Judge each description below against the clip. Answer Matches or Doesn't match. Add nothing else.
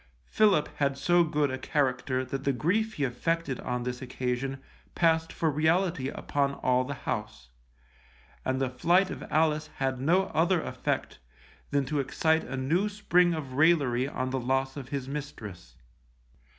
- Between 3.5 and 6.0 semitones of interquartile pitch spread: Matches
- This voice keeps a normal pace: Matches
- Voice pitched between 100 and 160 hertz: Matches